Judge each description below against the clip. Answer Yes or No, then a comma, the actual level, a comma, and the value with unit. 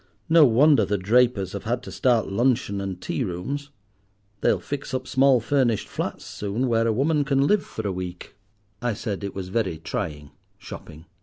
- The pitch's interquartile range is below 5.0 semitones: No, wide, 5.4 semitones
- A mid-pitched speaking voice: No, low, 115 Hz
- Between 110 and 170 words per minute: No, average, 180 wpm